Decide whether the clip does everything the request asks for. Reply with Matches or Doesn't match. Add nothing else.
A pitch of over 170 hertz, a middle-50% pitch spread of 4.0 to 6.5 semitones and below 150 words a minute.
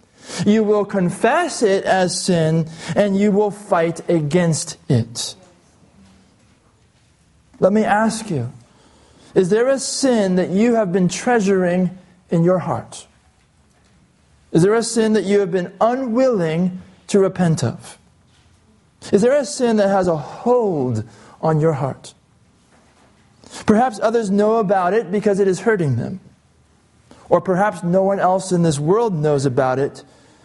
Matches